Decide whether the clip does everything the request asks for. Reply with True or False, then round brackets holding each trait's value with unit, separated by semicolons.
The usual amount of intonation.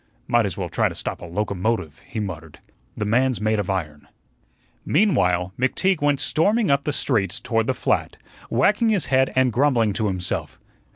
False (6.7 semitones)